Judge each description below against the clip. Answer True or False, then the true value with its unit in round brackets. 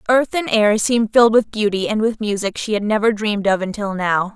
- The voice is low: False (215 Hz)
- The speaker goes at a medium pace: False (235 wpm)